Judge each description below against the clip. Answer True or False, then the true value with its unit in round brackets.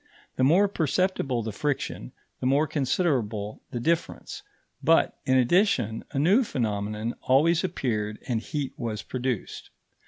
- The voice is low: True (130 Hz)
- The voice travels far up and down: True (5.9 semitones)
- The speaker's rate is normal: False (130 wpm)